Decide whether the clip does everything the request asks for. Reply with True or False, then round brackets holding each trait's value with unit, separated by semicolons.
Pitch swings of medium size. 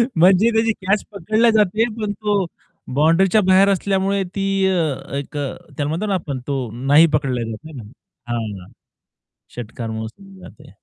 False (6.2 semitones)